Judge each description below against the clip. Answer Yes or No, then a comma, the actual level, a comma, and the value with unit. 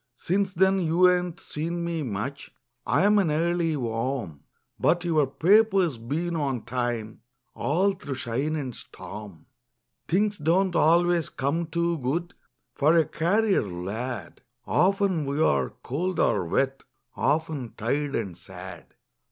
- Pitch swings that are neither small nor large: No, wide, 5.7 semitones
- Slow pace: Yes, slow, 130 wpm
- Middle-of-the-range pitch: Yes, medium, 155 Hz